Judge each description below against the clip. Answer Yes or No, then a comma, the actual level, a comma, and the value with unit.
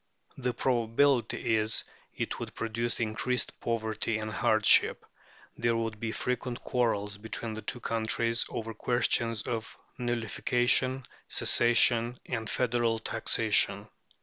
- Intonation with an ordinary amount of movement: No, narrow, 1.6 semitones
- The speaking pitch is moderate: No, low, 115 Hz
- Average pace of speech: No, slow, 120 wpm